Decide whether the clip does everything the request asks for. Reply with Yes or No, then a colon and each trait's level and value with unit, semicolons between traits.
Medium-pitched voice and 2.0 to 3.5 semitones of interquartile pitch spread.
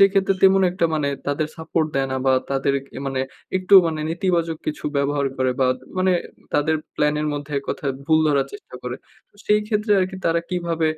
No: medium, 160 Hz; average, 4.6 semitones